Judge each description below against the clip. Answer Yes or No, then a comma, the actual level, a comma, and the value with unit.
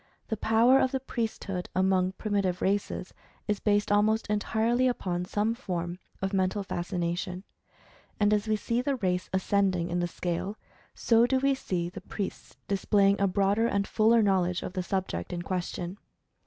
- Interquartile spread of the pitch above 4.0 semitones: No, average, 3.2 semitones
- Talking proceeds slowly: No, average, 170 wpm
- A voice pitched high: Yes, high, 200 Hz